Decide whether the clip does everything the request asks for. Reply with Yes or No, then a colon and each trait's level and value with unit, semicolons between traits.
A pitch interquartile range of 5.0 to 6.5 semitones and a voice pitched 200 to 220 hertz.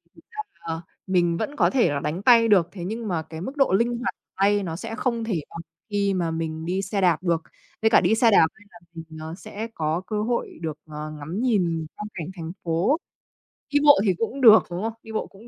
No: wide, 5.4 semitones; high, 190 Hz